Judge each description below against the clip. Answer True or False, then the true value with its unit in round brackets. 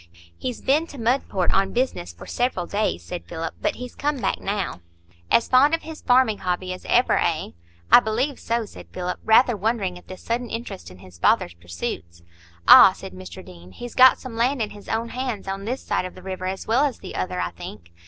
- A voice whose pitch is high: True (210 Hz)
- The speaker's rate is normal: False (210 wpm)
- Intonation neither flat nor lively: False (6.3 semitones)